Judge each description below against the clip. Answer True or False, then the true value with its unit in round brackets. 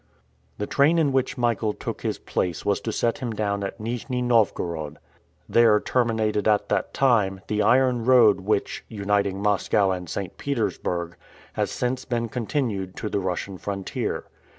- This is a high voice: False (105 Hz)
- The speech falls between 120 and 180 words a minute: True (155 wpm)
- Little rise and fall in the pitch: False (3.8 semitones)